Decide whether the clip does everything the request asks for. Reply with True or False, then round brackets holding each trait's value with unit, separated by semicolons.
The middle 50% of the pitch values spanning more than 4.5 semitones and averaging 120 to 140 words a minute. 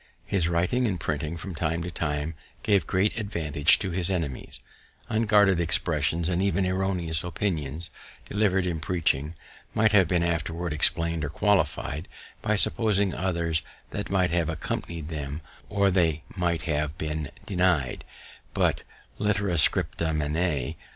False (3.4 semitones; 135 wpm)